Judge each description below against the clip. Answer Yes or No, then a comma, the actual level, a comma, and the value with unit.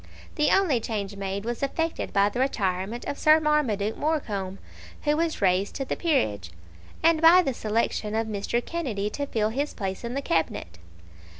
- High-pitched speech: Yes, high, 230 Hz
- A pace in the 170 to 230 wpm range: Yes, average, 175 wpm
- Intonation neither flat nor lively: No, wide, 7.0 semitones